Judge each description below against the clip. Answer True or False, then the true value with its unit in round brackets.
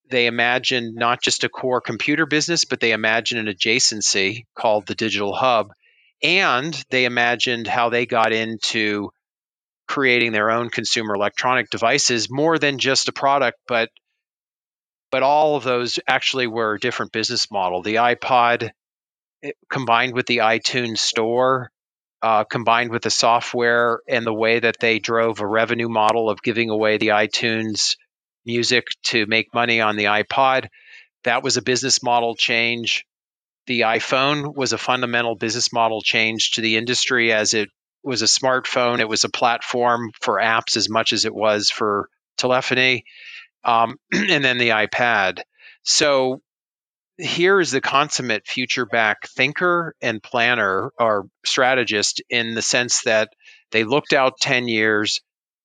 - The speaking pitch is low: True (120 Hz)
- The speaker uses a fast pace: False (150 wpm)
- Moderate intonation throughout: False (2.3 semitones)